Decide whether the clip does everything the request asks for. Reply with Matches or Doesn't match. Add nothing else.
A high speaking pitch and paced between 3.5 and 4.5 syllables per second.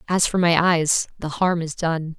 Doesn't match